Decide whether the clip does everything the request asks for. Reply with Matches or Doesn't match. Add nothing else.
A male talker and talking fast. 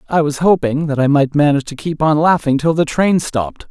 Matches